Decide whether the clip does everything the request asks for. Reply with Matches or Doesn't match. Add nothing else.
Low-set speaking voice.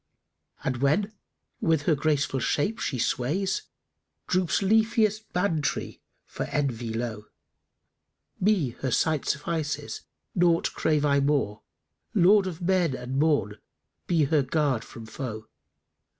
Doesn't match